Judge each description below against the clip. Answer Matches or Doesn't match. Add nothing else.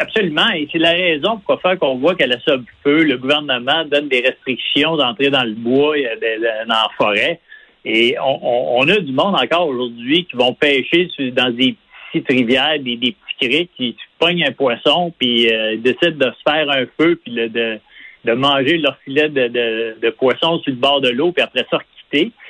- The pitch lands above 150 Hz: Doesn't match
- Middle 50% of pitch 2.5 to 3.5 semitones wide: Doesn't match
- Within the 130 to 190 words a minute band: Doesn't match